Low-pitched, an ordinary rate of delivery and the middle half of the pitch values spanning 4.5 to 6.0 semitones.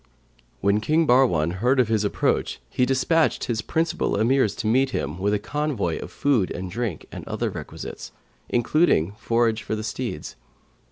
Yes: low, 115 Hz; average, 165 wpm; average, 4.8 semitones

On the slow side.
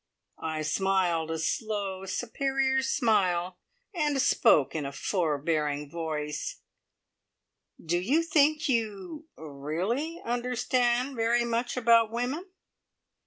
Yes: slow, 105 wpm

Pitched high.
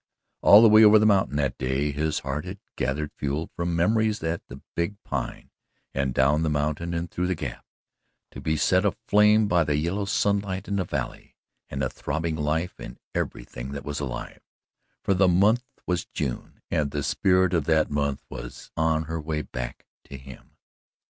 No: very low, 80 Hz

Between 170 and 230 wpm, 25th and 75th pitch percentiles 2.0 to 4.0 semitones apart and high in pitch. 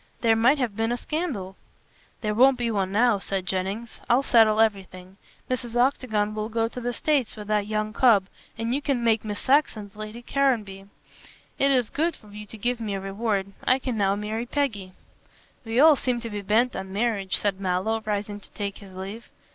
Yes: average, 195 wpm; average, 3.2 semitones; high, 220 Hz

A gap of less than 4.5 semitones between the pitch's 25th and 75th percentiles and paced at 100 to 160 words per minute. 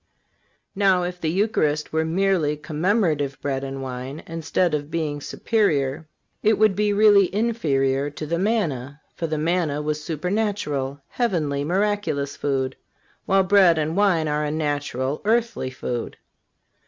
No: average, 5.3 semitones; average, 140 wpm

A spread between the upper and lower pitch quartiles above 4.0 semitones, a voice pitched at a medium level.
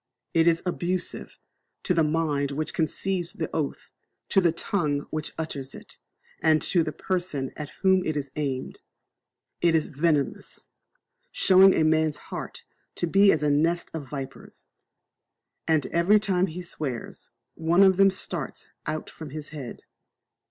No: average, 3.2 semitones; medium, 160 Hz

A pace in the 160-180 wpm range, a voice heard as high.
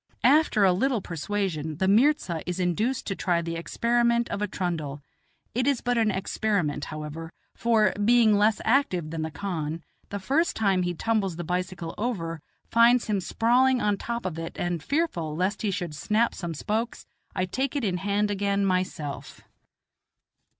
Yes: average, 170 wpm; high, 195 Hz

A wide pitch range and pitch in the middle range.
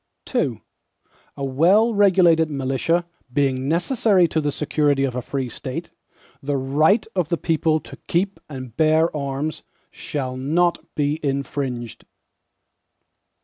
No: average, 3.9 semitones; medium, 150 Hz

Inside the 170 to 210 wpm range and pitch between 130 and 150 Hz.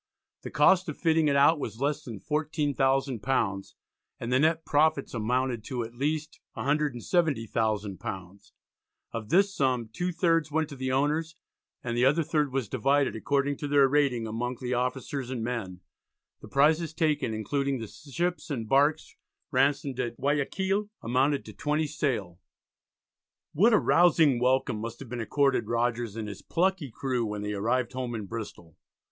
No: average, 155 wpm; low, 135 Hz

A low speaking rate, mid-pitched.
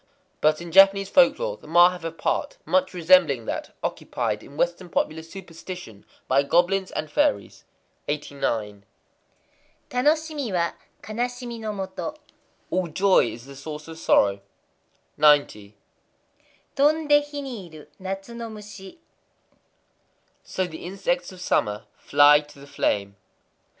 Yes: slow, 125 wpm; medium, 180 Hz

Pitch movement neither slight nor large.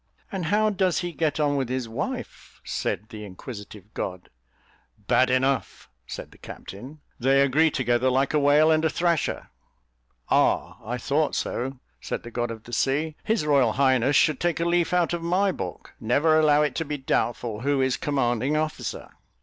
Yes: average, 4.5 semitones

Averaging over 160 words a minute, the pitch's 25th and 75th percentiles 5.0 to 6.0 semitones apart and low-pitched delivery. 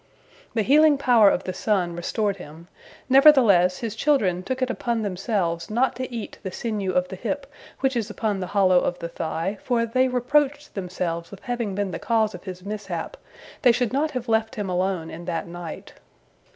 No: average, 190 wpm; average, 5.3 semitones; high, 210 Hz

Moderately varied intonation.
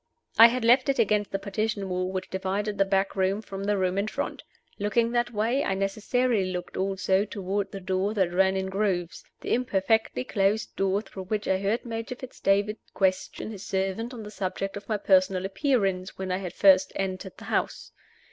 No: narrow, 2.2 semitones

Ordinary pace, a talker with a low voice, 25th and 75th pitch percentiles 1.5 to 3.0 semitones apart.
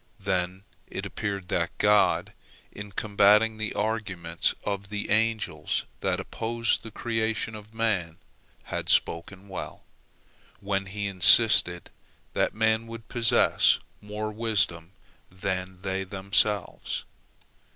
No: slow, 110 wpm; low, 105 Hz; average, 2.7 semitones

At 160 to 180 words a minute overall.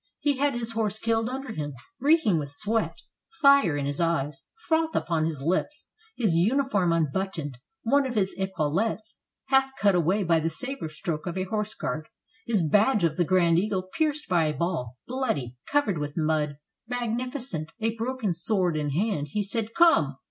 Yes: average, 175 wpm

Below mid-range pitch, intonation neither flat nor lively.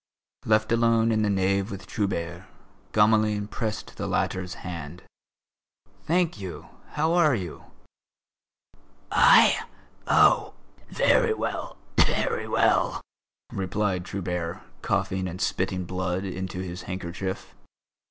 Yes: very low, 95 Hz; average, 3.0 semitones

